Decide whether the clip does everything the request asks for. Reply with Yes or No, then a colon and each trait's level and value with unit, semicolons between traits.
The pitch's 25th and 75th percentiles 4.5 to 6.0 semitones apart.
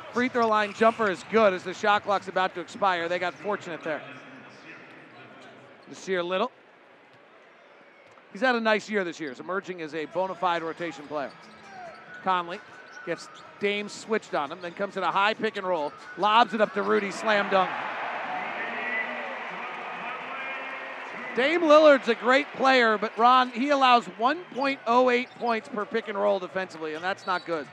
No: average, 4.1 semitones